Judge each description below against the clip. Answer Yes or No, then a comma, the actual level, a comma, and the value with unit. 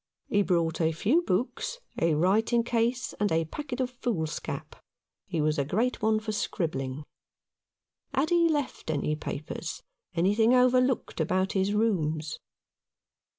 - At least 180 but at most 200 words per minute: No, average, 140 wpm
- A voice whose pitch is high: Yes, high, 205 Hz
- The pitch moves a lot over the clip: Yes, wide, 7.4 semitones